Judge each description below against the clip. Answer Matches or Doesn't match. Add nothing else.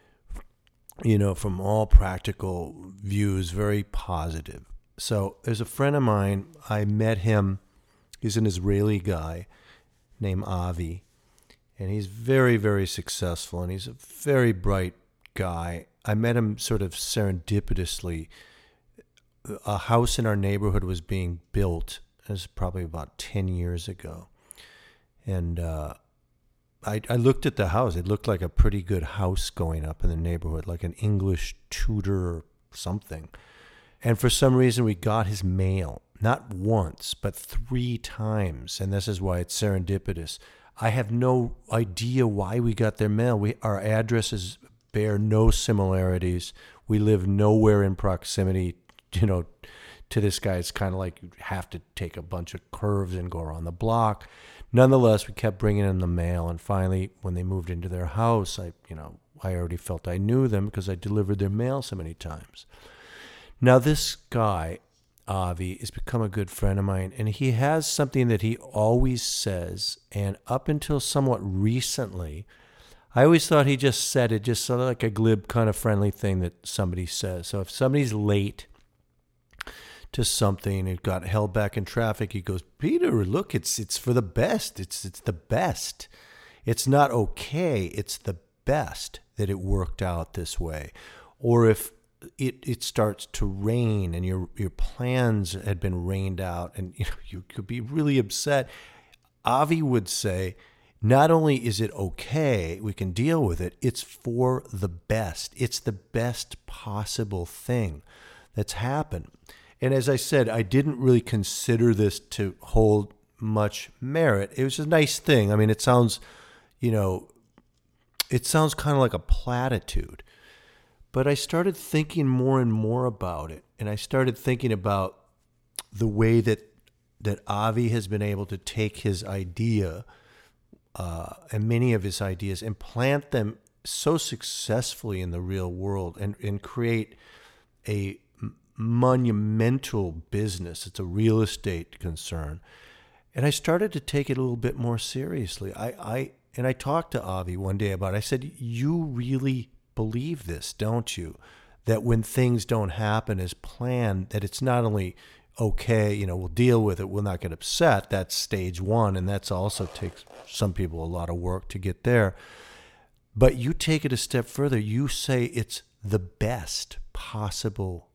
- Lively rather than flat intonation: Doesn't match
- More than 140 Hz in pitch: Doesn't match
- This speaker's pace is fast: Doesn't match